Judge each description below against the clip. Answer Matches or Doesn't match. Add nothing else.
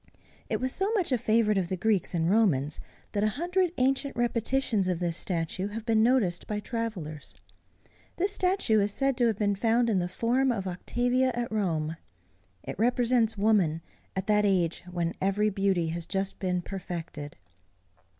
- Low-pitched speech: Doesn't match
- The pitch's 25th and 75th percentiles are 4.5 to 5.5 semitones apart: Matches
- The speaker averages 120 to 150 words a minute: Doesn't match